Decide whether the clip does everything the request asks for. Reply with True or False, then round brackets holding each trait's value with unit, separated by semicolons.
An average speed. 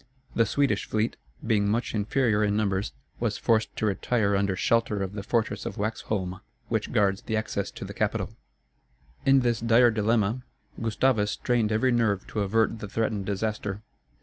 True (165 wpm)